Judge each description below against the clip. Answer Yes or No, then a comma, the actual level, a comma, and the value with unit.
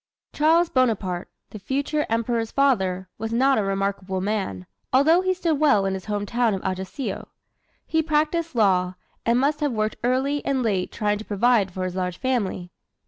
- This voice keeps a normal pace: Yes, average, 175 wpm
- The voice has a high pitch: Yes, high, 225 Hz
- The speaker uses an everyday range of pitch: No, wide, 6.4 semitones